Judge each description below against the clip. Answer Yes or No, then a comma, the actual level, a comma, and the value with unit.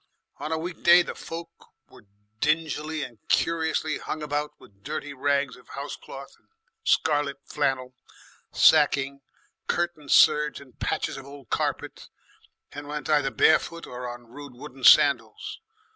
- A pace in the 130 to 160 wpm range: Yes, average, 140 wpm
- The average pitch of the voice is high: No, medium, 145 Hz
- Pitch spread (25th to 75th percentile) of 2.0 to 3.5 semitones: Yes, narrow, 2.5 semitones